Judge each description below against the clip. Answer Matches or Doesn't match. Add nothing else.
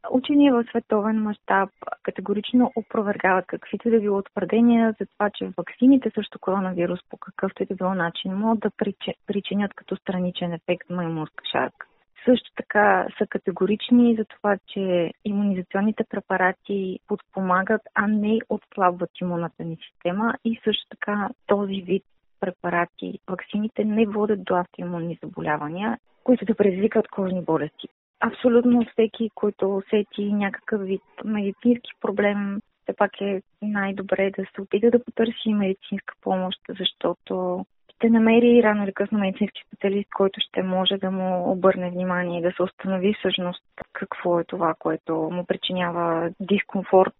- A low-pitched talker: Doesn't match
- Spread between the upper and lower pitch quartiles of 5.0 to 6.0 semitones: Doesn't match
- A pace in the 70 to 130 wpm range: Doesn't match